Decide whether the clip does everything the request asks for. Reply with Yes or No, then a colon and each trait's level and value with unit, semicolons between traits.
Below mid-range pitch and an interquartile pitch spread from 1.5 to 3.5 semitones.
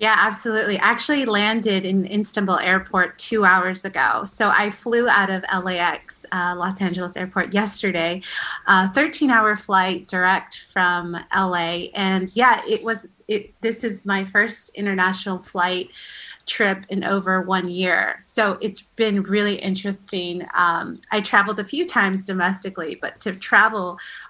No: high, 195 Hz; narrow, 2.6 semitones